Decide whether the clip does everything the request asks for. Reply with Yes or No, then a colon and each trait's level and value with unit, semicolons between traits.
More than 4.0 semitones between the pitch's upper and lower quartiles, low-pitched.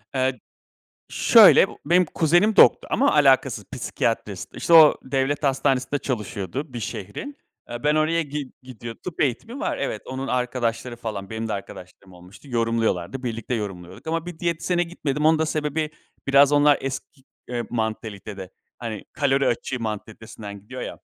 Yes: average, 5.3 semitones; low, 130 Hz